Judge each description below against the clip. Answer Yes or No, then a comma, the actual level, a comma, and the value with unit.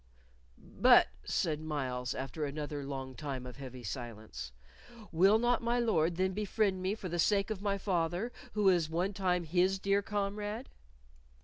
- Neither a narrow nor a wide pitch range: No, wide, 6.0 semitones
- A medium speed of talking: Yes, average, 155 wpm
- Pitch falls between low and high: Yes, medium, 180 Hz